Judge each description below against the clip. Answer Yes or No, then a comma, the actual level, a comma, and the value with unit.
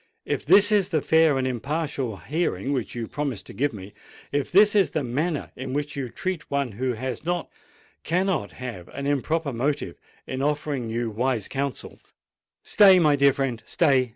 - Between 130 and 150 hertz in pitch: Yes, medium, 140 Hz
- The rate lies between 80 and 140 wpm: No, average, 165 wpm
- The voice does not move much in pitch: No, average, 4.1 semitones